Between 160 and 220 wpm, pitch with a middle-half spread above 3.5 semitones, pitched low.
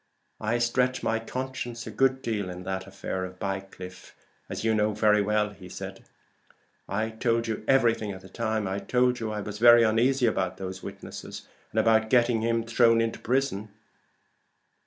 No: average, 165 wpm; average, 2.7 semitones; low, 110 Hz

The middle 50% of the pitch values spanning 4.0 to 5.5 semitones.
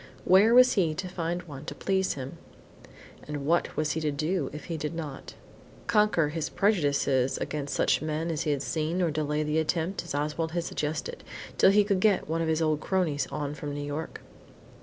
No: average, 3.2 semitones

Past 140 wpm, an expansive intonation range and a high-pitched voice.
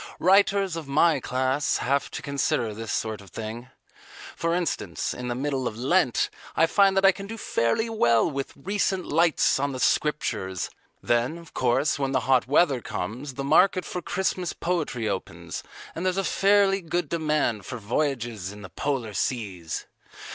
No: average, 170 wpm; wide, 6.7 semitones; medium, 140 Hz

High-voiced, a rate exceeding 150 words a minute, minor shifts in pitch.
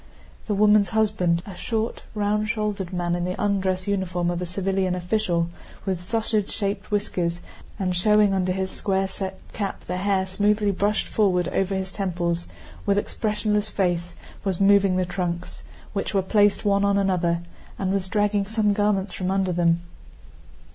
Yes: high, 195 Hz; average, 160 wpm; narrow, 2.3 semitones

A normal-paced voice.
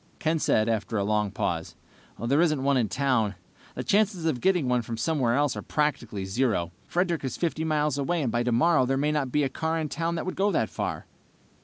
No: fast, 220 wpm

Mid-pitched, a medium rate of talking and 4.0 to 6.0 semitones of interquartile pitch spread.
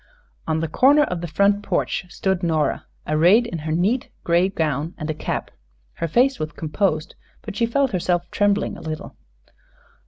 Yes: medium, 175 Hz; average, 175 wpm; average, 4.4 semitones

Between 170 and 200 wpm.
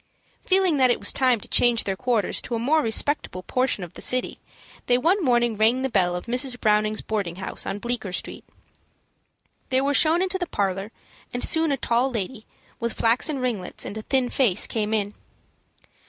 Yes: average, 190 wpm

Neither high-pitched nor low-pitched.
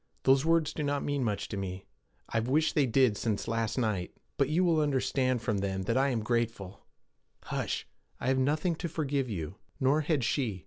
No: low, 130 Hz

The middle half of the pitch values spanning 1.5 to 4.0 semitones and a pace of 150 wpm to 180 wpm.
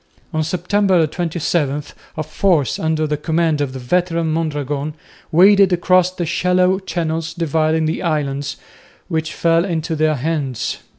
No: narrow, 2.6 semitones; slow, 135 wpm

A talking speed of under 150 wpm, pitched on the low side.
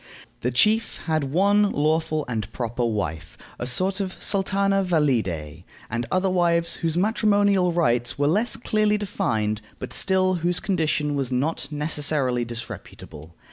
No: average, 140 wpm; medium, 160 Hz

